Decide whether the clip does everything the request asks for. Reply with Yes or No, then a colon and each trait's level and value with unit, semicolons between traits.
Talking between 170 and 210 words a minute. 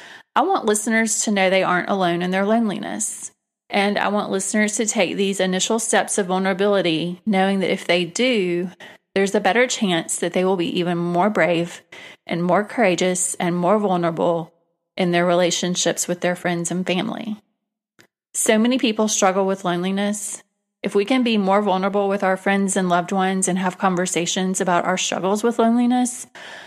Yes: average, 175 wpm